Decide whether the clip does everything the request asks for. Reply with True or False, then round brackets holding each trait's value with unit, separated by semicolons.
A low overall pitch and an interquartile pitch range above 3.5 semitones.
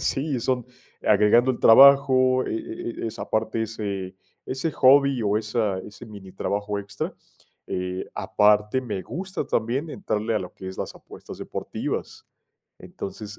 True (110 Hz; 4.1 semitones)